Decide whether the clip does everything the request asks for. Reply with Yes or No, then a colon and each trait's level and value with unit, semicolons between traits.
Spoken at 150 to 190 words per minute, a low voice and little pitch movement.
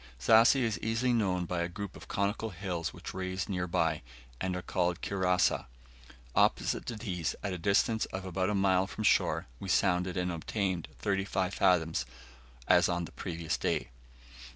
Yes: average, 170 wpm; very low, 95 Hz; narrow, 2.3 semitones